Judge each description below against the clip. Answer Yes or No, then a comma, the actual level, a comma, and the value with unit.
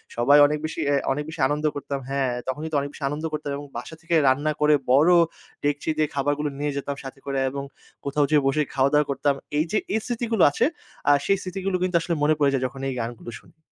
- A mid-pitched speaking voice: Yes, medium, 145 Hz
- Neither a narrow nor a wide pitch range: No, narrow, 2.1 semitones